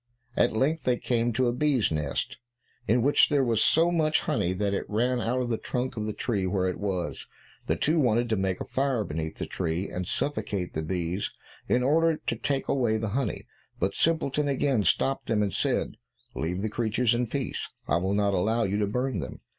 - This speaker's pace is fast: Yes, fast, 210 wpm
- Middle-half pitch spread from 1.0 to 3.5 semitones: No, average, 5.1 semitones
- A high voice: No, low, 115 Hz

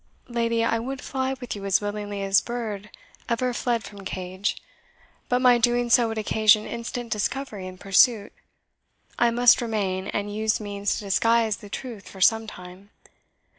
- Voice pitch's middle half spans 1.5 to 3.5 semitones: Yes, average, 2.9 semitones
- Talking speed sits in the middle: Yes, average, 165 wpm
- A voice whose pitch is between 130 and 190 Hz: No, high, 220 Hz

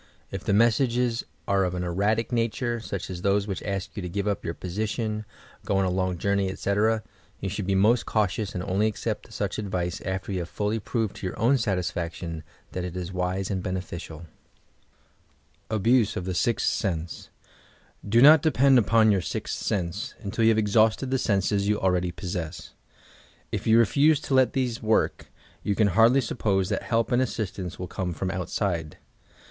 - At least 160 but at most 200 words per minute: Yes, average, 185 wpm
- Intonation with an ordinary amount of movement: Yes, average, 3.5 semitones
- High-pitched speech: No, low, 100 Hz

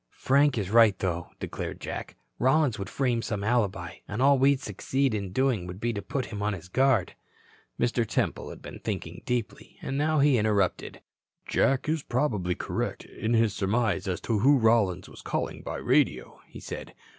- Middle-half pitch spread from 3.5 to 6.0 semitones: Yes, average, 4.9 semitones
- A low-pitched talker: Yes, low, 115 Hz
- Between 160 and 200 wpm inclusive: Yes, average, 180 wpm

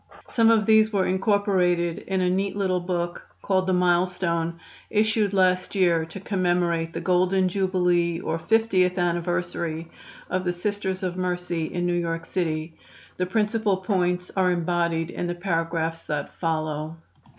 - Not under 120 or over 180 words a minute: Yes, average, 150 wpm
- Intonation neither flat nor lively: No, narrow, 1.9 semitones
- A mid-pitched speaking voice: Yes, medium, 180 Hz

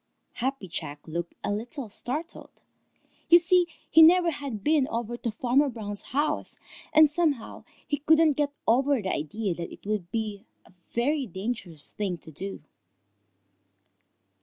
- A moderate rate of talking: Yes, average, 145 wpm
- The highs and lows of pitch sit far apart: Yes, wide, 6.7 semitones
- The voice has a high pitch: Yes, high, 240 Hz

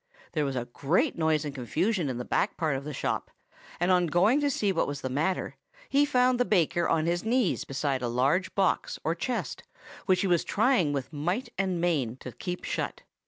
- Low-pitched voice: No, medium, 170 Hz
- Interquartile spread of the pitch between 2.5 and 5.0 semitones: No, wide, 5.6 semitones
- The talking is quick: Yes, fast, 210 wpm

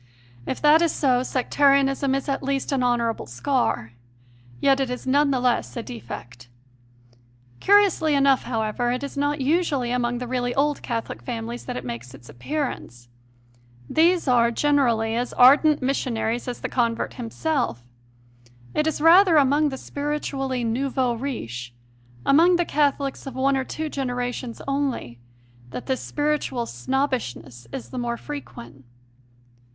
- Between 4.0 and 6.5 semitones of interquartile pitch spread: No, average, 3.5 semitones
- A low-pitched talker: No, very high, 260 Hz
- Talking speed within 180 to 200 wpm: No, average, 150 wpm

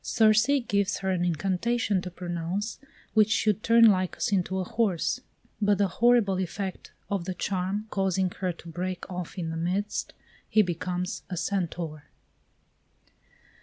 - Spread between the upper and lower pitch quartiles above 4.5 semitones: No, narrow, 2.5 semitones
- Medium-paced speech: Yes, average, 145 wpm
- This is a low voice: No, high, 190 Hz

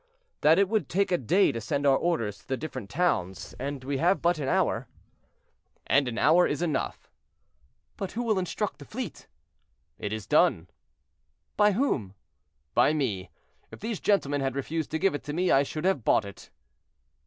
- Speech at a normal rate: Yes, average, 185 wpm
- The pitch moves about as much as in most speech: No, wide, 5.8 semitones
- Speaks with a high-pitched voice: No, medium, 150 Hz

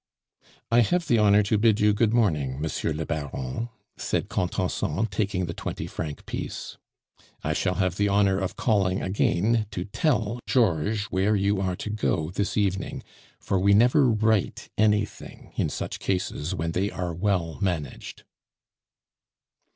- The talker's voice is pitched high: No, low, 100 Hz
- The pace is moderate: Yes, average, 150 wpm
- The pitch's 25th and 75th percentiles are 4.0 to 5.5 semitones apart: No, average, 3.3 semitones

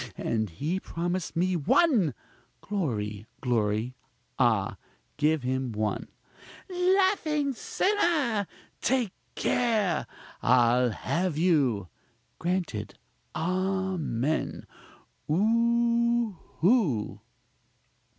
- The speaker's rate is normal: No, slow, 75 wpm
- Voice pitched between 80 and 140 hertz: No, medium, 175 Hz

